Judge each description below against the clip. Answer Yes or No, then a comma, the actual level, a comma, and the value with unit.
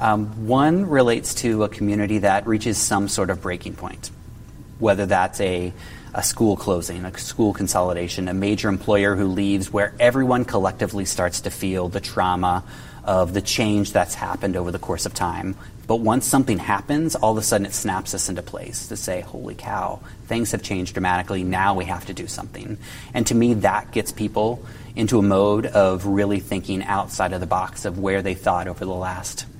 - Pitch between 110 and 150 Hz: No, low, 100 Hz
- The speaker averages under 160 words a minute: No, average, 195 wpm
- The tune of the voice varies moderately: Yes, average, 3.0 semitones